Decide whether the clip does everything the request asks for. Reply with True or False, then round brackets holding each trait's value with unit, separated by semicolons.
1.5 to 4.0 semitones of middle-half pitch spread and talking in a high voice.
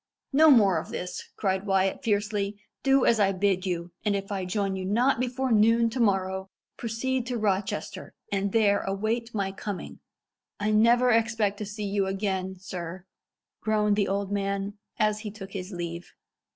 True (2.6 semitones; 205 Hz)